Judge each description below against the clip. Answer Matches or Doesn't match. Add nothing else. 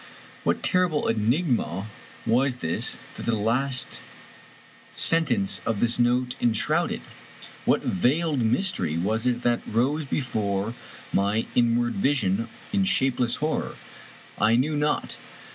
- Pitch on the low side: Matches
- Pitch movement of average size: Matches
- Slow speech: Matches